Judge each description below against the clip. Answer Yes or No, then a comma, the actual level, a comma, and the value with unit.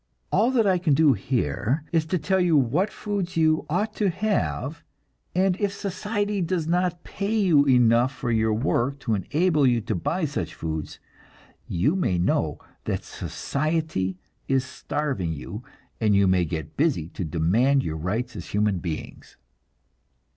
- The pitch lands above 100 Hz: Yes, medium, 140 Hz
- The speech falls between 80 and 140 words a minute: No, average, 160 wpm